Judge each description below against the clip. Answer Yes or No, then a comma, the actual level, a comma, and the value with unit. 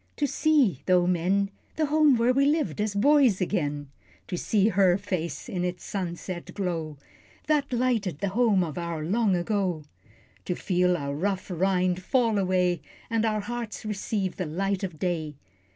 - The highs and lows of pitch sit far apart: No, average, 4.0 semitones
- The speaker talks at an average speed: Yes, average, 165 wpm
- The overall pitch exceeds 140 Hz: Yes, high, 190 Hz